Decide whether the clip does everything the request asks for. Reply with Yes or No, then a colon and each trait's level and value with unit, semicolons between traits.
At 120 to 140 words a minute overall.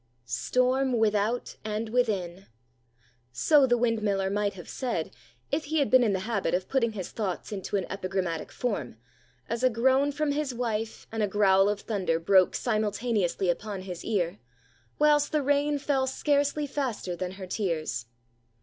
No: average, 160 wpm